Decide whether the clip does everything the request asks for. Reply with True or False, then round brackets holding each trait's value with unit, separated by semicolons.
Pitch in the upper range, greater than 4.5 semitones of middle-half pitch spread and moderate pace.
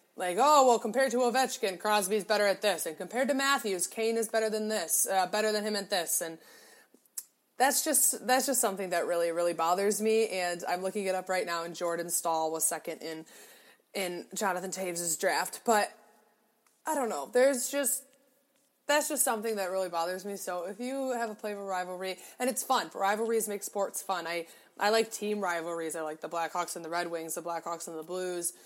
False (205 Hz; 5.4 semitones; 210 wpm)